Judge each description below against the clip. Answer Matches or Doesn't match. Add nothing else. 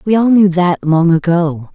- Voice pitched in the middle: Matches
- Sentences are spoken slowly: Doesn't match